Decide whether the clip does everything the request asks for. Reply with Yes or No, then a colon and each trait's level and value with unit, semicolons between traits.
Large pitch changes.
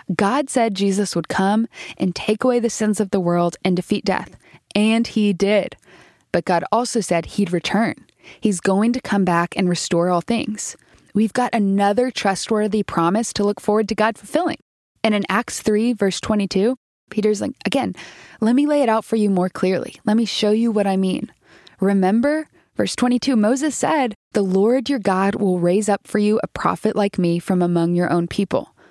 No: average, 3.0 semitones